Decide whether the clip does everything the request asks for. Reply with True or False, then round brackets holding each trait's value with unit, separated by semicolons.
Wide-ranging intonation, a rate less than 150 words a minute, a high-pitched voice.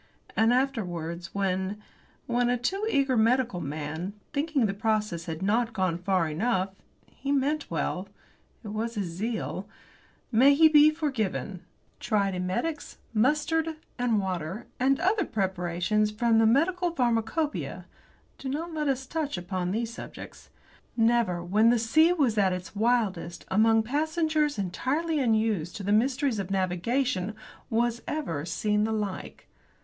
True (6.3 semitones; 140 wpm; 225 Hz)